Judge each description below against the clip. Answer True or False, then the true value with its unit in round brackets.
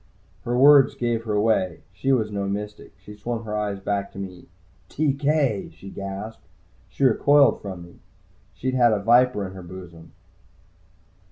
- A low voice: True (105 Hz)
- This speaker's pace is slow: False (160 wpm)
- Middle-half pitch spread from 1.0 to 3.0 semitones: False (4.2 semitones)